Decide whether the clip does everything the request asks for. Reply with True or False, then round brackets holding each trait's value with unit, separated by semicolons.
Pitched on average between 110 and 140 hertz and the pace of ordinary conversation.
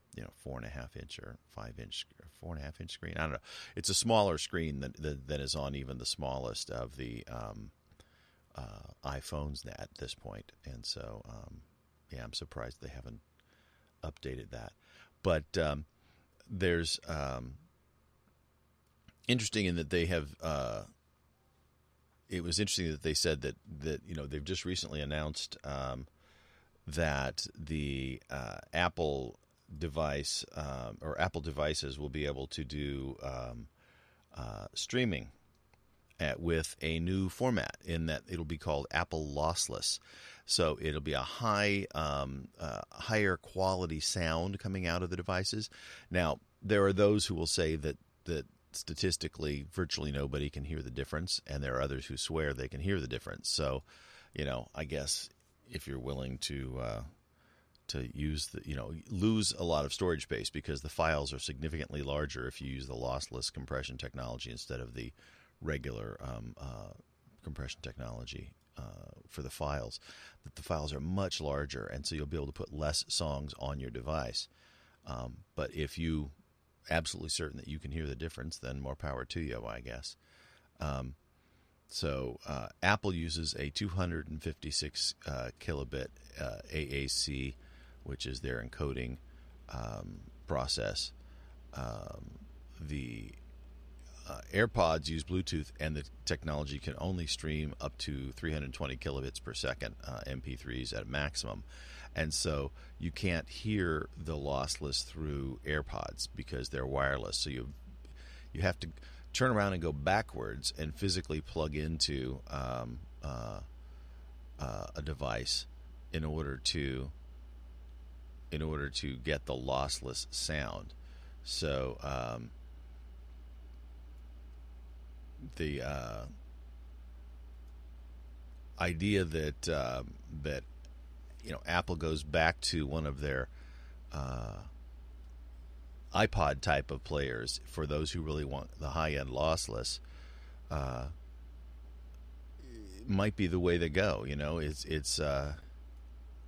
False (70 Hz; 145 wpm)